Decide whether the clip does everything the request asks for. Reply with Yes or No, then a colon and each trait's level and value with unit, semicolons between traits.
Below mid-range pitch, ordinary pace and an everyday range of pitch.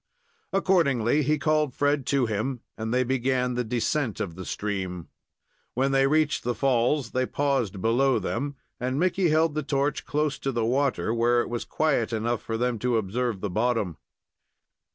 Yes: low, 125 Hz; average, 175 wpm; average, 3.7 semitones